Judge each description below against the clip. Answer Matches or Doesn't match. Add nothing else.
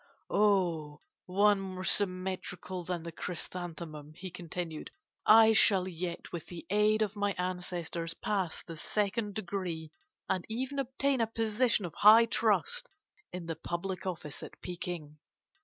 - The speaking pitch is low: Doesn't match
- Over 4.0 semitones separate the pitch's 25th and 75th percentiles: Doesn't match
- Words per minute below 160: Matches